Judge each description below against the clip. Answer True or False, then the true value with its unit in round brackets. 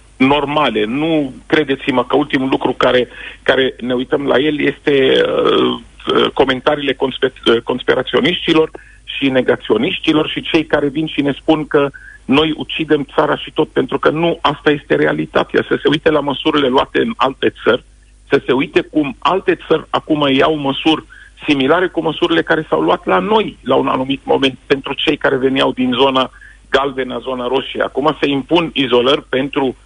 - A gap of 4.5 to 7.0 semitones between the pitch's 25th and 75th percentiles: False (3.0 semitones)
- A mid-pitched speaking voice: True (145 Hz)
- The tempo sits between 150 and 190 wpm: True (170 wpm)